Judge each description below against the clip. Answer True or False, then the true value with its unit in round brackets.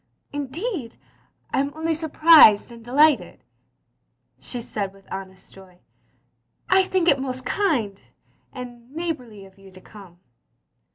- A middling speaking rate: True (150 wpm)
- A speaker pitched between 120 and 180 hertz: False (245 Hz)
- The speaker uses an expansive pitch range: True (7.9 semitones)